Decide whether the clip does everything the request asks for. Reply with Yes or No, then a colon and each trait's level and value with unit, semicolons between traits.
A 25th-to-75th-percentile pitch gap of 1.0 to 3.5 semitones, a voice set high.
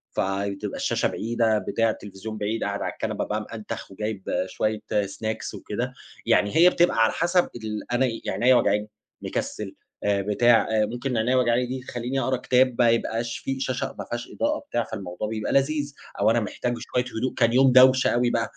No: average, 3.1 semitones; low, 115 Hz